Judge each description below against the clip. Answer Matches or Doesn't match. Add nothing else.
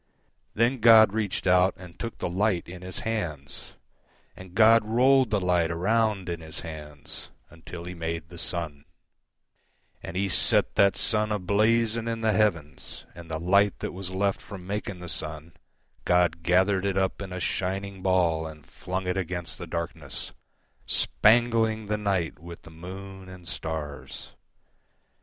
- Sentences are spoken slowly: Doesn't match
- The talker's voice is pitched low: Matches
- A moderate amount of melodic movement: Matches